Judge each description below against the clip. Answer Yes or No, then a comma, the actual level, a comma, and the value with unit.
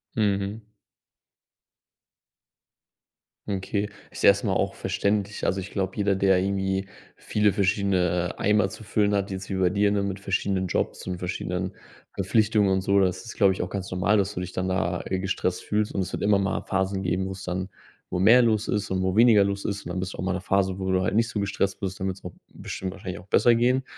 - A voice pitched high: No, very low, 95 Hz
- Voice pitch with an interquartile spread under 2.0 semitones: Yes, narrow, 1.5 semitones